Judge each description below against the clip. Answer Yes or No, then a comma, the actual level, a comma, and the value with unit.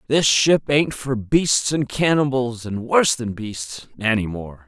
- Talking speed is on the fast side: No, average, 165 wpm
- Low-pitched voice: Yes, low, 120 Hz